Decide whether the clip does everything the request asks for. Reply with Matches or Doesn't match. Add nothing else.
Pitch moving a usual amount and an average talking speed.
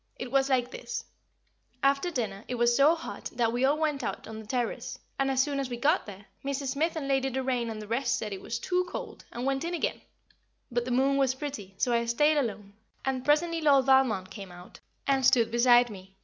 Doesn't match